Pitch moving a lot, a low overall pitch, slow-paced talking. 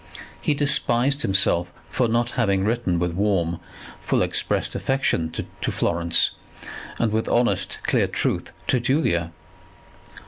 Yes: wide, 6.0 semitones; low, 110 Hz; slow, 125 wpm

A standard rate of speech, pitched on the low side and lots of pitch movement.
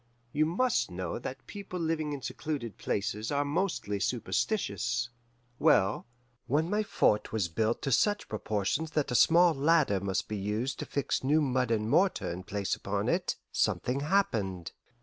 Yes: average, 160 wpm; low, 130 Hz; wide, 7.2 semitones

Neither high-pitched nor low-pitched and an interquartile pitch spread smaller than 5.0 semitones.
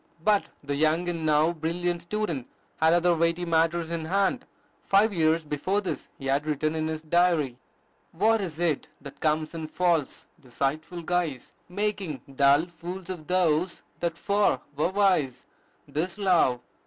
Yes: medium, 165 Hz; average, 2.7 semitones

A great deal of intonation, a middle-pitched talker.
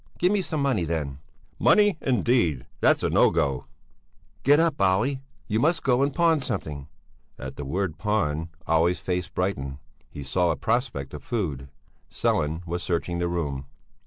No: wide, 8.9 semitones; very low, 90 Hz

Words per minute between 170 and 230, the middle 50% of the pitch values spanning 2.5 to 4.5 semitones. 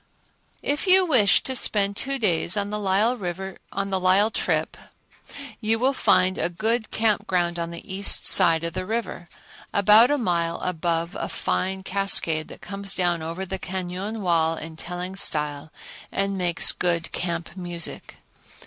No: average, 150 wpm; average, 3.3 semitones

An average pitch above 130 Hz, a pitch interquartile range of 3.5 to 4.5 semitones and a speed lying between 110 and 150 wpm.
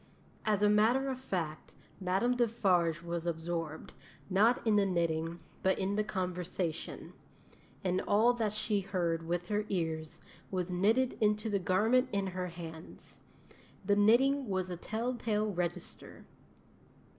Yes: high, 190 Hz; average, 3.8 semitones; average, 140 wpm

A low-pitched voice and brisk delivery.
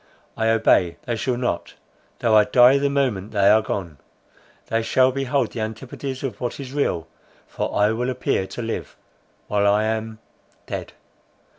No: low, 115 Hz; average, 150 wpm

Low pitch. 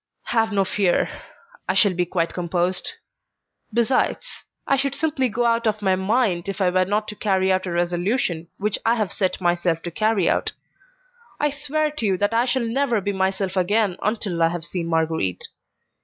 No: high, 195 Hz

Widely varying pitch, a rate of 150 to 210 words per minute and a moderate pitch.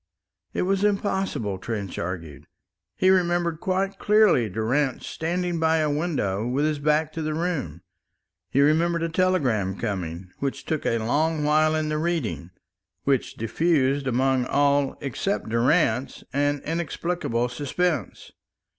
No: wide, 6.1 semitones; slow, 135 wpm; medium, 150 Hz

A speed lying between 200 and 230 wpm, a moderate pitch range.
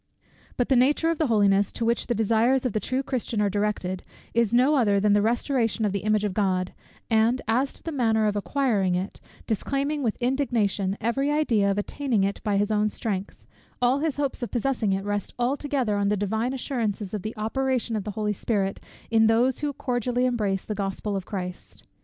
Yes: fast, 205 wpm; average, 3.8 semitones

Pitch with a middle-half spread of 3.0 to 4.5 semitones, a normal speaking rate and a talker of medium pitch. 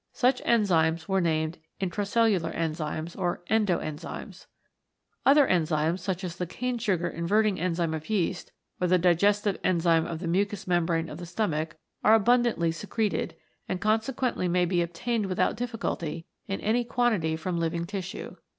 Yes: average, 4.2 semitones; average, 155 wpm; medium, 180 Hz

